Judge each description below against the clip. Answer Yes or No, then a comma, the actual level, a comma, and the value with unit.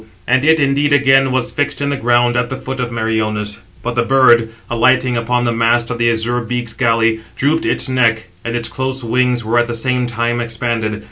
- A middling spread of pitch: No, narrow, 2.1 semitones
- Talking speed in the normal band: No, fast, 210 wpm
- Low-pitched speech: Yes, low, 120 Hz